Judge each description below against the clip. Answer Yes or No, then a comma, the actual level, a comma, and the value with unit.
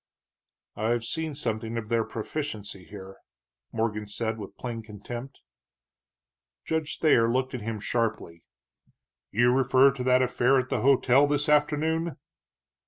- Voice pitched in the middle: No, low, 120 Hz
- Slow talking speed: Yes, slow, 130 wpm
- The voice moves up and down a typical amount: Yes, average, 3.8 semitones